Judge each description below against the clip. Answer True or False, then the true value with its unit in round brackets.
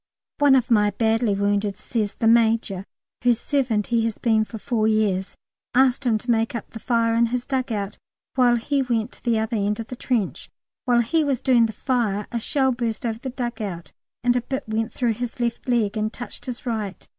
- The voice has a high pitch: True (230 Hz)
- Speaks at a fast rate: True (215 wpm)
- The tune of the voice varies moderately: False (2.2 semitones)